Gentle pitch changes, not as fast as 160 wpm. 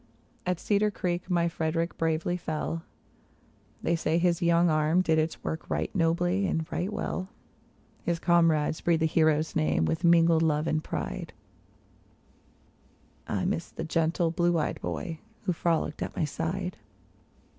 Yes: narrow, 1.6 semitones; average, 145 wpm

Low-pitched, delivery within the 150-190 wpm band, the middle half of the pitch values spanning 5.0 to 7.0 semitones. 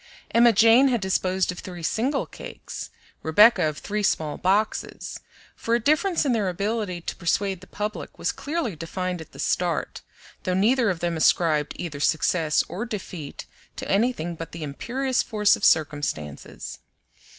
No: high, 190 Hz; average, 160 wpm; wide, 5.6 semitones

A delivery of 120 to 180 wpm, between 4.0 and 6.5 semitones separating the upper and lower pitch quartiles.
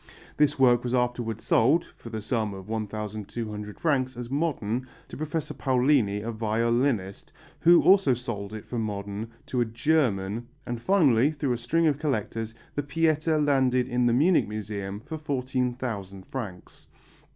Yes: average, 150 wpm; average, 4.7 semitones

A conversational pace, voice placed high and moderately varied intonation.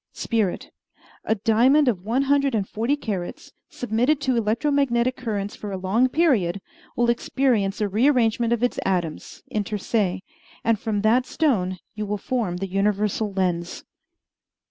Yes: average, 150 wpm; high, 220 Hz; average, 4.1 semitones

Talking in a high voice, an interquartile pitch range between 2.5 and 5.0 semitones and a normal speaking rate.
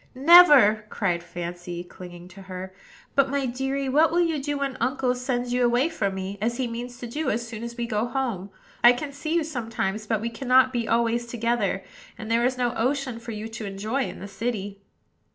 No: high, 235 Hz; average, 3.7 semitones; fast, 210 wpm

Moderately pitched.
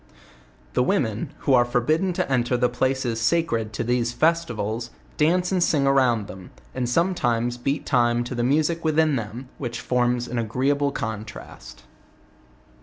No: low, 125 Hz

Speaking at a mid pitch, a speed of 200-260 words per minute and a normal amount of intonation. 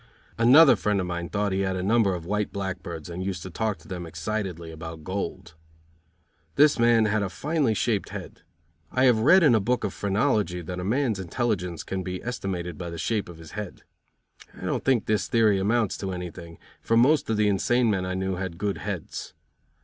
No: low, 100 Hz; fast, 205 wpm; average, 3.9 semitones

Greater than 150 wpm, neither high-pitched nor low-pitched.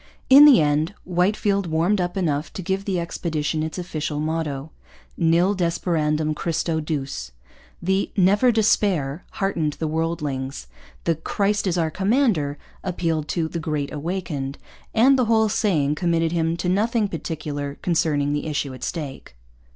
No: average, 145 wpm; medium, 165 Hz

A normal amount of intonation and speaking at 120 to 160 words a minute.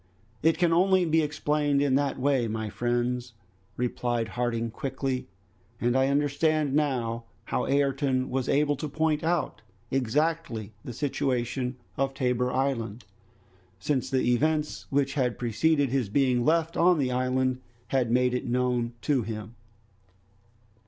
Yes: average, 3.3 semitones; average, 140 wpm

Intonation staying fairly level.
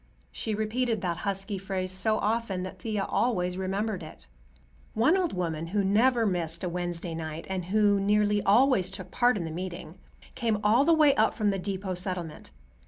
No: average, 3.3 semitones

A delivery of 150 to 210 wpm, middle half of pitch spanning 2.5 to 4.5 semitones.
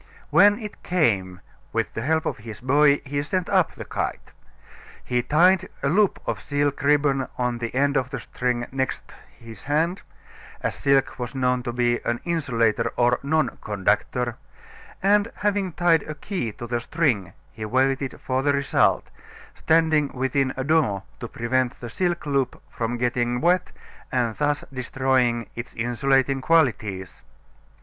Yes: average, 155 wpm; average, 4.0 semitones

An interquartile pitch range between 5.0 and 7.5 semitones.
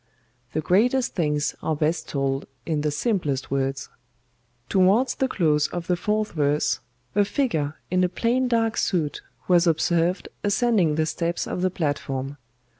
Yes: wide, 5.5 semitones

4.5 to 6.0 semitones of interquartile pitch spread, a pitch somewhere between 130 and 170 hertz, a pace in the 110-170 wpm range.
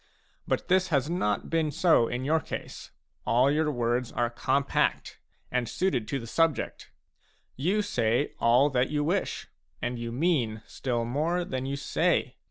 Yes: average, 5.1 semitones; low, 135 Hz; average, 160 wpm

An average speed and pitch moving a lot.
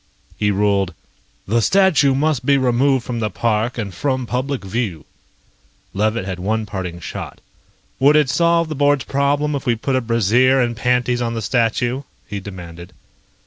No: average, 165 wpm; average, 4.7 semitones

